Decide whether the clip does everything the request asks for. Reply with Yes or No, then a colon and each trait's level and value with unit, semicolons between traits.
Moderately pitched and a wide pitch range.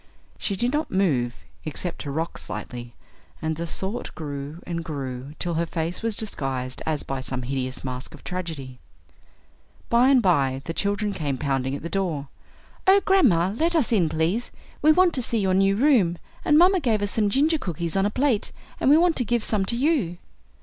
Yes: medium, 180 Hz; wide, 8.6 semitones